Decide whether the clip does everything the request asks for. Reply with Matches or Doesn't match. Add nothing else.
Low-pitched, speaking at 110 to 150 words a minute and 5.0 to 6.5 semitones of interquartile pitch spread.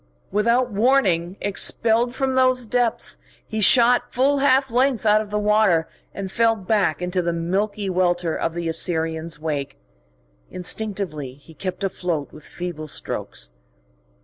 Doesn't match